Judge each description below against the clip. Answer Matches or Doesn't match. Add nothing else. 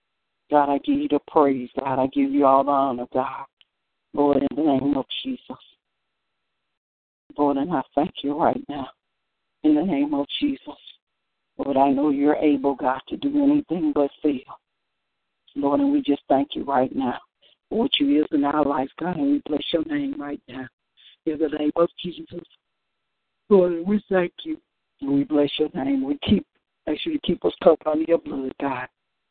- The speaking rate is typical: Matches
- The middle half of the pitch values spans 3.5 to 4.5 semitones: Matches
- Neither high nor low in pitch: Matches